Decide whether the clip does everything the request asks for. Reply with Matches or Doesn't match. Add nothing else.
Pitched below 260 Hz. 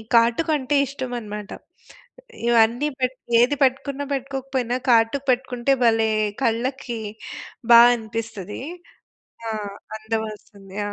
Matches